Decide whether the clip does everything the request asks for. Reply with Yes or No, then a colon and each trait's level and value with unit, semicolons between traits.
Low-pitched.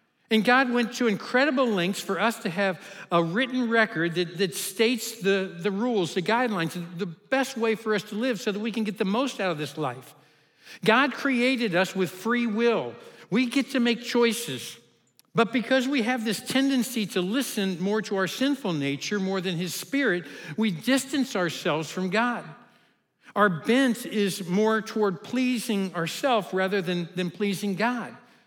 No: high, 215 Hz